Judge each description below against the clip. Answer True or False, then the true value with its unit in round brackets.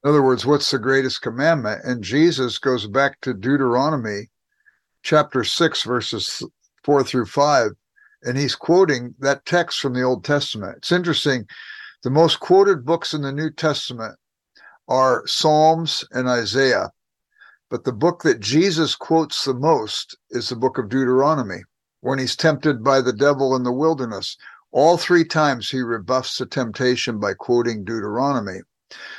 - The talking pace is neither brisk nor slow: True (150 wpm)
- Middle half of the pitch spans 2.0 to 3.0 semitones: False (3.8 semitones)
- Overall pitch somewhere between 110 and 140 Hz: True (135 Hz)